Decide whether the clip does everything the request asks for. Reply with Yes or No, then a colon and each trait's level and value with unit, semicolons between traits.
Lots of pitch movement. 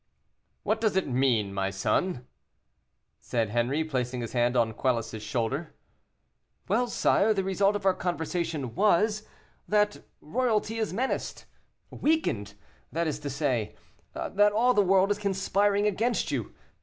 Yes: wide, 9.0 semitones